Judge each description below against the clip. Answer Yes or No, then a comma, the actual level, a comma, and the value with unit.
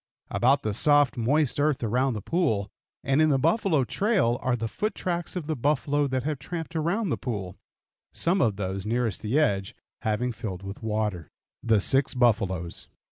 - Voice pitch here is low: Yes, low, 125 Hz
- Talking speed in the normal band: Yes, average, 180 wpm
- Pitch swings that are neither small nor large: No, wide, 6.2 semitones